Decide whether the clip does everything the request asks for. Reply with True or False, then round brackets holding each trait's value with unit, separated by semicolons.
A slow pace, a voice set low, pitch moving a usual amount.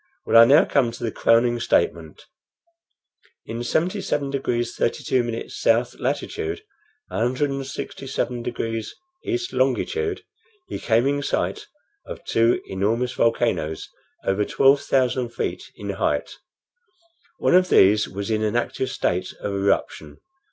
True (125 wpm; 120 Hz; 3.4 semitones)